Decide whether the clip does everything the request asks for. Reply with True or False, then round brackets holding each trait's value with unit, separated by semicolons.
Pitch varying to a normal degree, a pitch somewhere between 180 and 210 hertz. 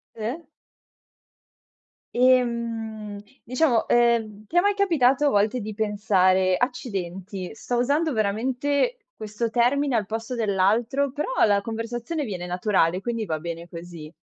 False (3.9 semitones; 225 Hz)